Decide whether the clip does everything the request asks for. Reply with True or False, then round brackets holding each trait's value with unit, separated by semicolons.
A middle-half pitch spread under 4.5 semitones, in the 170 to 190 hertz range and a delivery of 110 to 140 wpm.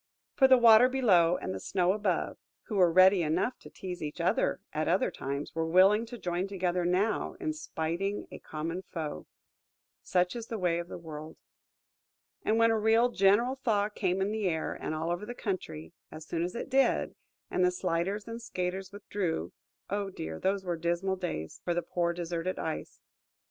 False (3.7 semitones; 185 Hz; 185 wpm)